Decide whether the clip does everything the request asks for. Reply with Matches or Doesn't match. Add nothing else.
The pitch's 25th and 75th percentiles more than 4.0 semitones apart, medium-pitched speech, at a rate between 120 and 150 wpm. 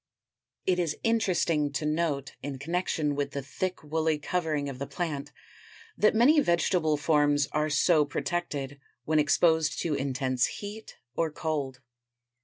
Doesn't match